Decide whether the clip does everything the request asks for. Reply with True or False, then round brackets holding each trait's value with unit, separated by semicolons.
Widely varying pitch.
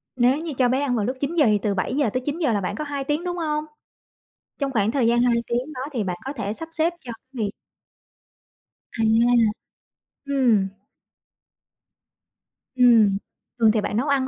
False (4.4 semitones)